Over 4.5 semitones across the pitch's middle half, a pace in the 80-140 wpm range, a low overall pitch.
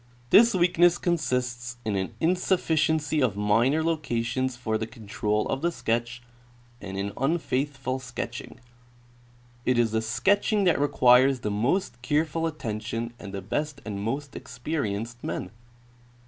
Yes: wide, 5.6 semitones; slow, 135 wpm; low, 125 Hz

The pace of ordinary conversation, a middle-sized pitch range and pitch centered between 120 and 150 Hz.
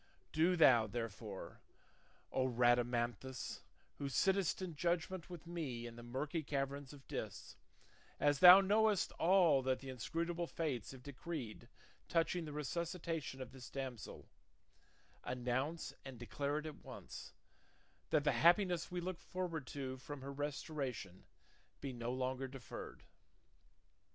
No: slow, 130 wpm; average, 4.9 semitones; medium, 140 Hz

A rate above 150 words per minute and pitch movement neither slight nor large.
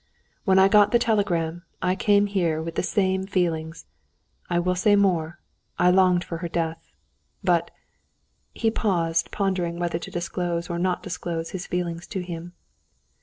No: average, 165 wpm; narrow, 2.2 semitones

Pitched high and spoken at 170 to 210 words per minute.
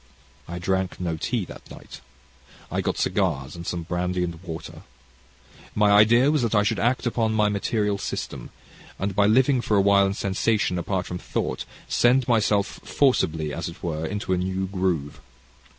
No: low, 100 Hz; average, 175 wpm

